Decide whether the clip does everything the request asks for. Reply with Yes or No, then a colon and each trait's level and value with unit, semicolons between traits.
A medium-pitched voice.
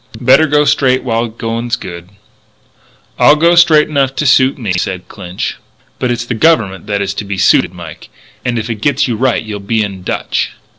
No: low, 120 Hz